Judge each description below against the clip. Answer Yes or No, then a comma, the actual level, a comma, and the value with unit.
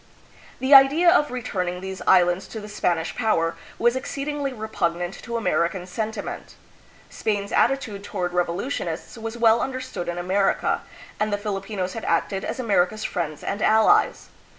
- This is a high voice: Yes, high, 205 Hz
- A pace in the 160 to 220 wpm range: No, average, 145 wpm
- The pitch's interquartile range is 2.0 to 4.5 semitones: No, average, 4.9 semitones